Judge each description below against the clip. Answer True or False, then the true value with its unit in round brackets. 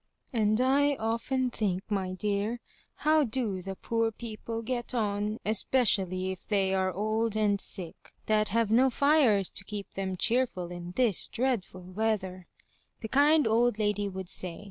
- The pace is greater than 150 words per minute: True (160 wpm)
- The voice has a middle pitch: False (215 Hz)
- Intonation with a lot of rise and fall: False (3.7 semitones)